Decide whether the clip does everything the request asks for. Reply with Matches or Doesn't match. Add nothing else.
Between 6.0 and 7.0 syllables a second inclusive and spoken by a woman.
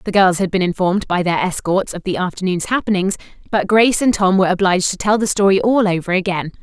Matches